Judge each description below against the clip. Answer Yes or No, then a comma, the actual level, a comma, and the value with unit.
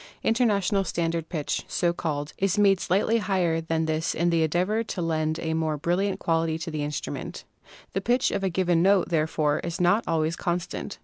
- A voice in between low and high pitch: Yes, medium, 170 Hz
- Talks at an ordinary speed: Yes, average, 185 wpm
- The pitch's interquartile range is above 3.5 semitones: No, average, 3.2 semitones